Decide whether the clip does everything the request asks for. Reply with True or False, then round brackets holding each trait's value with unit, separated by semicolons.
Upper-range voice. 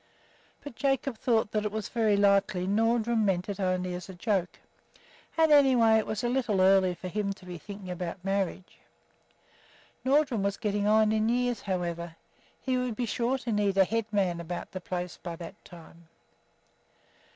True (205 Hz)